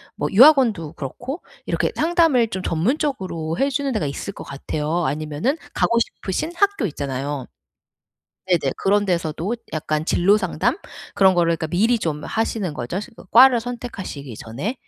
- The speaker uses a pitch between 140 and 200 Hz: Yes, high, 190 Hz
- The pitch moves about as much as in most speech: No, wide, 7.8 semitones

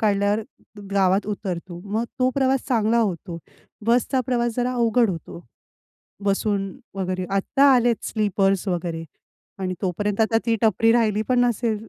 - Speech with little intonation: No, average, 3.4 semitones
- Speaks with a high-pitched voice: Yes, high, 210 Hz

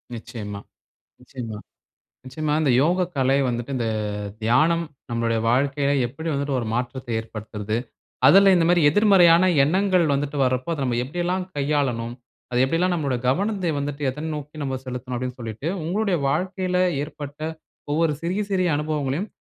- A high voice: No, medium, 140 Hz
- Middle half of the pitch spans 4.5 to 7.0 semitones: Yes, average, 5.2 semitones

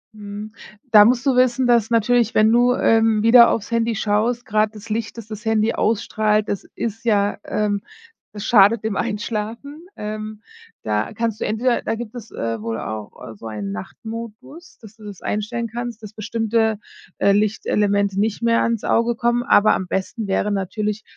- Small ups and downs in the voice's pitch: Yes, narrow, 2.0 semitones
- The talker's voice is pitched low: No, high, 215 Hz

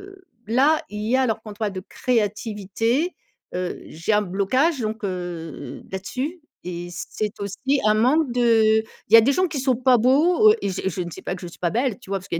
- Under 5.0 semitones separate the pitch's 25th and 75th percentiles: No, average, 5.3 semitones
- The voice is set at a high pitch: Yes, high, 220 Hz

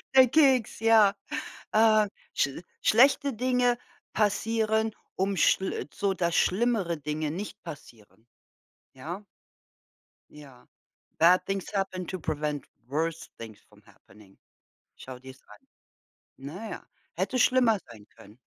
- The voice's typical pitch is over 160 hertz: Yes, medium, 185 Hz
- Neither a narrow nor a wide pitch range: No, wide, 7.1 semitones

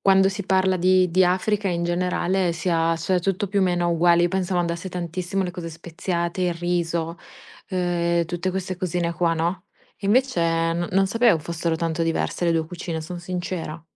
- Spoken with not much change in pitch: Yes, narrow, 1.7 semitones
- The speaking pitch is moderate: Yes, medium, 175 Hz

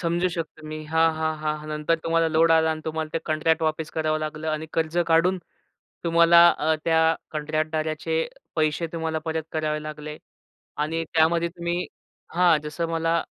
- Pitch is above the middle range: No, medium, 160 Hz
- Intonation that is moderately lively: No, narrow, 1.1 semitones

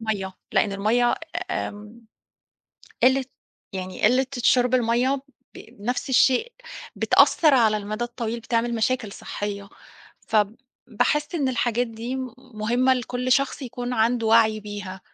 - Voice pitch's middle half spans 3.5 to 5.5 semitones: No, average, 2.9 semitones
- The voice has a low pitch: No, high, 235 Hz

